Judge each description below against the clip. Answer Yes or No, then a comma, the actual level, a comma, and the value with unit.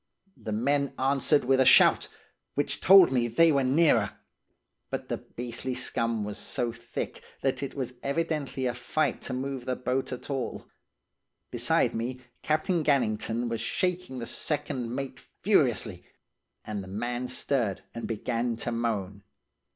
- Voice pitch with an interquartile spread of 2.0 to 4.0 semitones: Yes, average, 3.1 semitones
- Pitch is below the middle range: Yes, low, 125 Hz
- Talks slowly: No, average, 150 wpm